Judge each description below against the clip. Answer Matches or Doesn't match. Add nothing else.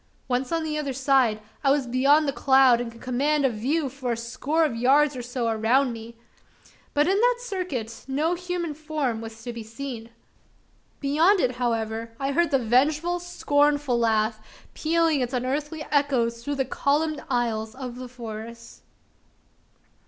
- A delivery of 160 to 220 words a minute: Matches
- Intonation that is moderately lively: Matches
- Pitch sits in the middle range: Doesn't match